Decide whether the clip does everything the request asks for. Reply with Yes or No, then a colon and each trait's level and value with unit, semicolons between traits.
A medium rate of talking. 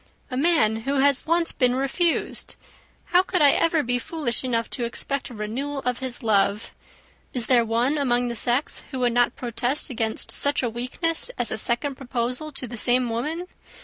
Yes: average, 185 wpm